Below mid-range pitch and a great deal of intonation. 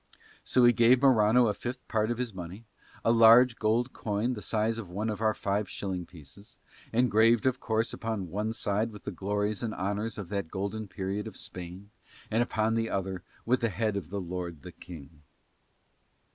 No: low, 105 Hz; average, 2.9 semitones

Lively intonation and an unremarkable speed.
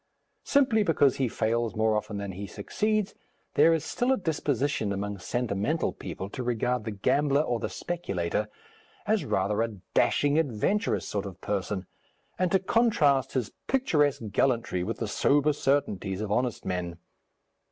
Yes: wide, 6.8 semitones; average, 150 wpm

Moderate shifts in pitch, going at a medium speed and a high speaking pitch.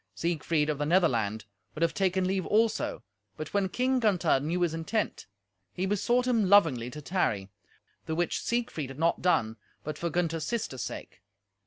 No: average, 4.8 semitones; average, 170 wpm; medium, 170 Hz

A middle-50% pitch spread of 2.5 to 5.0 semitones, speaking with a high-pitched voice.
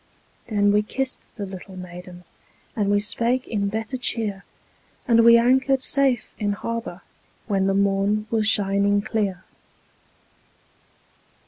Yes: average, 2.8 semitones; high, 210 Hz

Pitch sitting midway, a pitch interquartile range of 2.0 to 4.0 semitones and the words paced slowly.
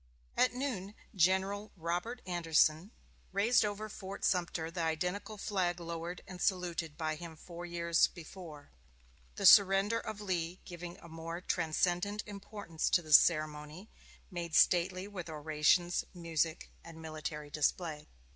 Yes: medium, 175 Hz; average, 3.0 semitones; slow, 130 wpm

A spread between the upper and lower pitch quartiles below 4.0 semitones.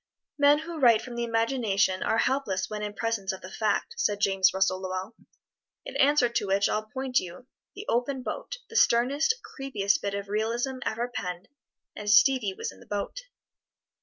No: average, 4.8 semitones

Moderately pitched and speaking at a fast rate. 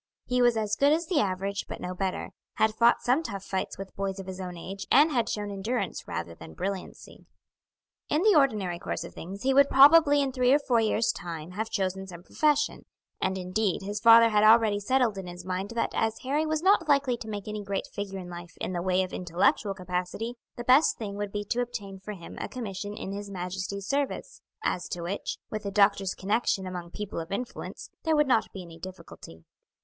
No: high, 205 Hz; fast, 215 wpm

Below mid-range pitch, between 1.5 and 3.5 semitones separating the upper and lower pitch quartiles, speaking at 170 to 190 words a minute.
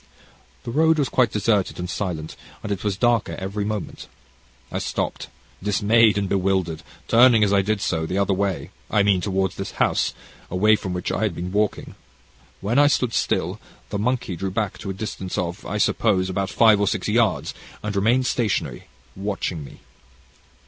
Yes: low, 100 Hz; narrow, 2.5 semitones; average, 180 wpm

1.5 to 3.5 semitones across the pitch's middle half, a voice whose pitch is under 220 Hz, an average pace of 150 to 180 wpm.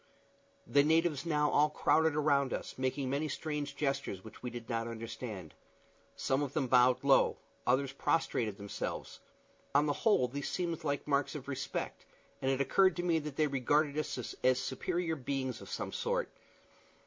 Yes: average, 3.0 semitones; medium, 140 Hz; average, 170 wpm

